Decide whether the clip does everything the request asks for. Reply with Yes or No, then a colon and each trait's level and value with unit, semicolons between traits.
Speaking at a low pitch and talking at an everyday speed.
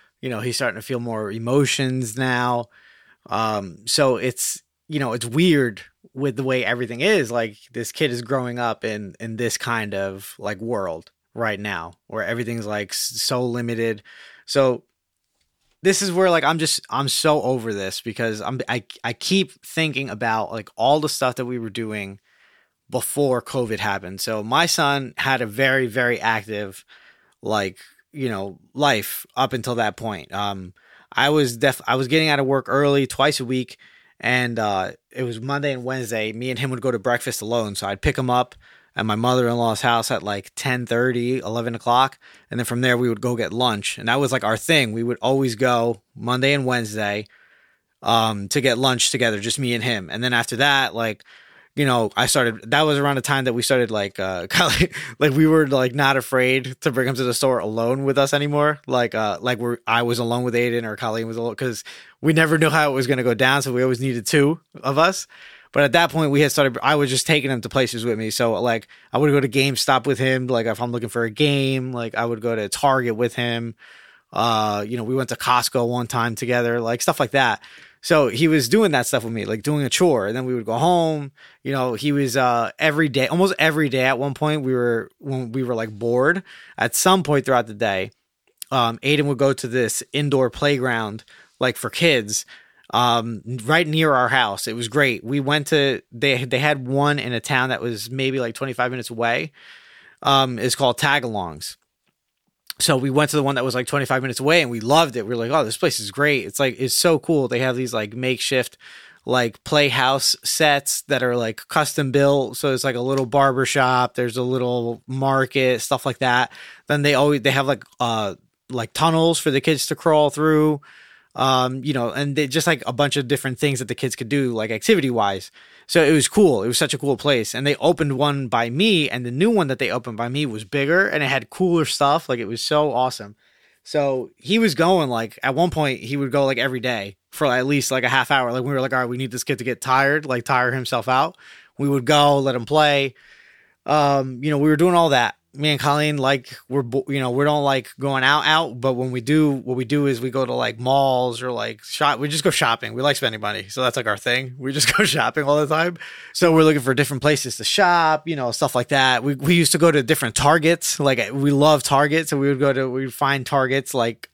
No: low, 130 Hz; fast, 230 wpm